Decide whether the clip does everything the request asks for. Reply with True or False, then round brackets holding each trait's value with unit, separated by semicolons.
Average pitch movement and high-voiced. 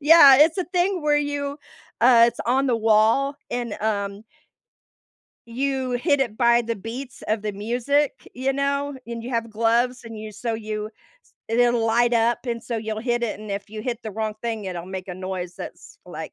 True (3.6 semitones; 235 Hz)